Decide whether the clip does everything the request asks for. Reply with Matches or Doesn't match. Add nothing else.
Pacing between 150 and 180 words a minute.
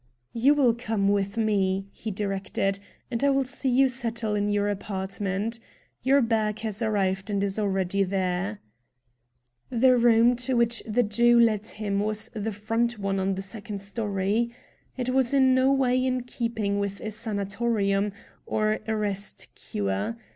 Matches